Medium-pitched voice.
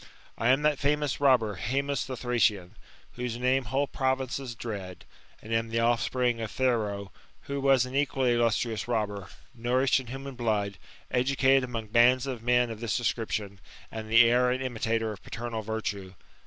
No: low, 120 Hz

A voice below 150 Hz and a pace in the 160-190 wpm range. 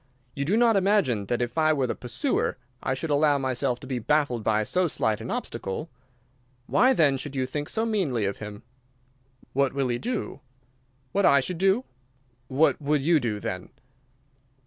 Yes: medium, 140 Hz; average, 180 wpm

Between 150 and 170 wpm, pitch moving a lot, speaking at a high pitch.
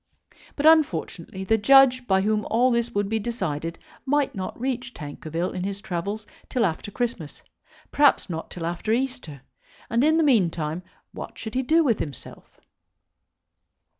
Yes: average, 155 wpm; wide, 6.5 semitones; high, 215 Hz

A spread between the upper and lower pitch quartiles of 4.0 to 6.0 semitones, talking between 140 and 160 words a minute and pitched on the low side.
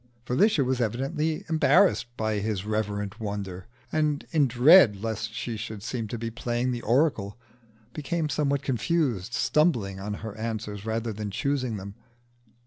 Yes: average, 5.0 semitones; average, 145 wpm; low, 115 Hz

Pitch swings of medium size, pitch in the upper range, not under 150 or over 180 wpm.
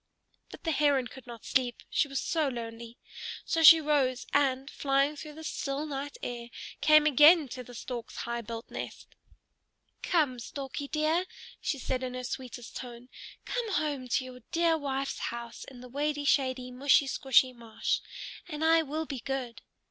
Yes: average, 3.2 semitones; very high, 270 Hz; average, 170 wpm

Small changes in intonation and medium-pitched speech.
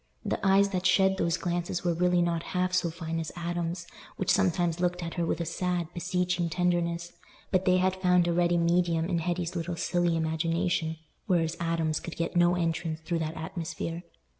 Yes: narrow, 1.3 semitones; medium, 175 Hz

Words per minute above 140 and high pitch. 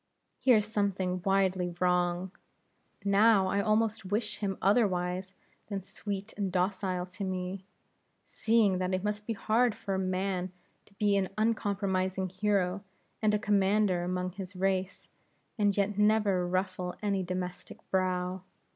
No: slow, 135 wpm; high, 195 Hz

